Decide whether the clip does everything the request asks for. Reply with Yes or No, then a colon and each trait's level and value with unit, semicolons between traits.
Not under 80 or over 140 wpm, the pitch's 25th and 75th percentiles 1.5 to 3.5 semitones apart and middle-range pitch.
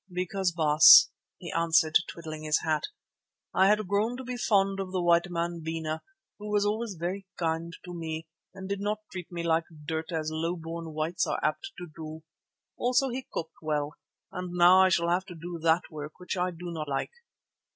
No: average, 195 wpm; average, 2.9 semitones; medium, 170 Hz